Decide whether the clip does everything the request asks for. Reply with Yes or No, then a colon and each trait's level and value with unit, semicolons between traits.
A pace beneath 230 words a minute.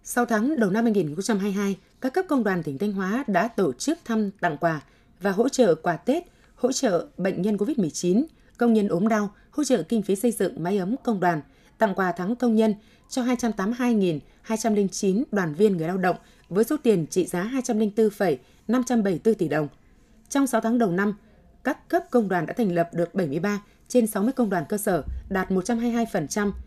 Yes: average, 190 wpm